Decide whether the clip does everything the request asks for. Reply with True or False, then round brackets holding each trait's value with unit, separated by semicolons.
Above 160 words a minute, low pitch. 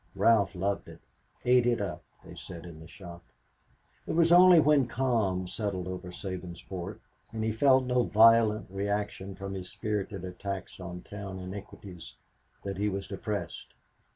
False (155 wpm; 100 Hz)